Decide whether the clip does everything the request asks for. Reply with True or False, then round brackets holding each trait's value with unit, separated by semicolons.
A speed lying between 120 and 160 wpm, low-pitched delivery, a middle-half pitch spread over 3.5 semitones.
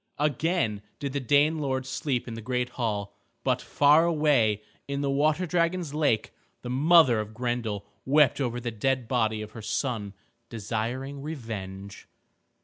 True (150 wpm; 125 Hz; 4.8 semitones)